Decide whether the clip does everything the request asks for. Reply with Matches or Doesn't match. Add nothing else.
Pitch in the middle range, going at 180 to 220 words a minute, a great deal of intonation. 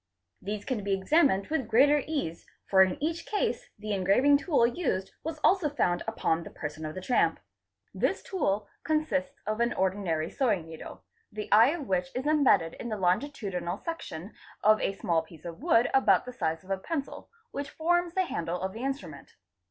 Doesn't match